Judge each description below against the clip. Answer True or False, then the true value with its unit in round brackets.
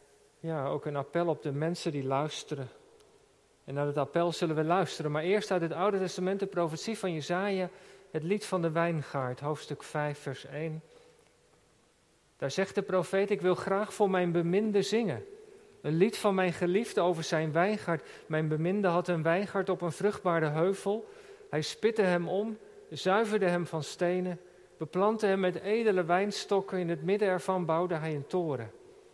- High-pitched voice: False (180 Hz)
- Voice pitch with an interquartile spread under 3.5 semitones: False (3.8 semitones)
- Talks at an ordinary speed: True (175 wpm)